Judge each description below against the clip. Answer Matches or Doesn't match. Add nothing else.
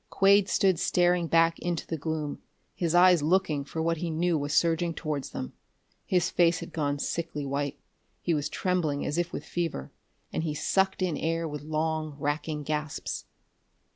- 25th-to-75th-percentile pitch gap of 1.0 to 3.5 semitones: Matches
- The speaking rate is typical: Matches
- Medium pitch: Matches